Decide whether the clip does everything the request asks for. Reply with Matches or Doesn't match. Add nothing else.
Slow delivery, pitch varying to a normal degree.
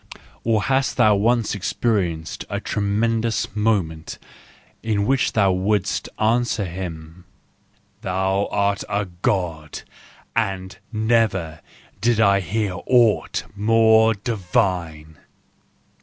Matches